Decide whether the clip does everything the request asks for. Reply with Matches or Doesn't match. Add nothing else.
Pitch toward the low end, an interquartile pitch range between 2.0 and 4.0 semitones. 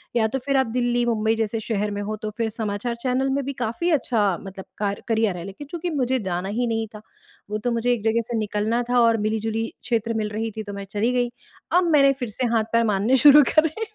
Doesn't match